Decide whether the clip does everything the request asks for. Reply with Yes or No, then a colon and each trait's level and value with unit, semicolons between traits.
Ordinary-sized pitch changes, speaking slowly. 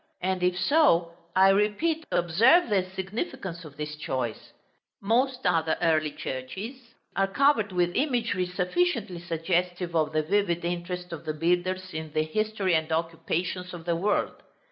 No: average, 3.9 semitones; average, 145 wpm